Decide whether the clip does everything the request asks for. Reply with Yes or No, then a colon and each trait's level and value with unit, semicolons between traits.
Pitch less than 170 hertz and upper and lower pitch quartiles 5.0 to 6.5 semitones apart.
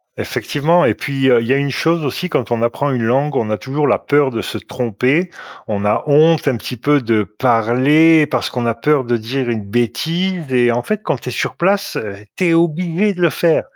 Yes: low, 135 Hz; wide, 5.4 semitones